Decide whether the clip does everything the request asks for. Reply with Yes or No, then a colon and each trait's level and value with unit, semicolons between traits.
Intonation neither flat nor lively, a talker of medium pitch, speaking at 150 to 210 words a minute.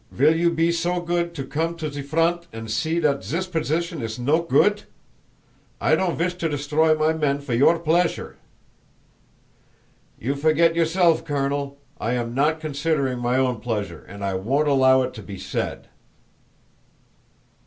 Yes: average, 4.0 semitones; medium, 150 Hz; average, 160 wpm